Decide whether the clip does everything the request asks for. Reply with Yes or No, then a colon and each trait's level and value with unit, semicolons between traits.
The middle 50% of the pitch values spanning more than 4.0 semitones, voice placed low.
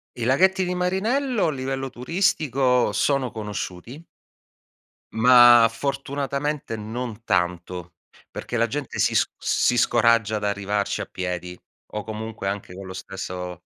Yes: average, 5.3 semitones; low, 115 Hz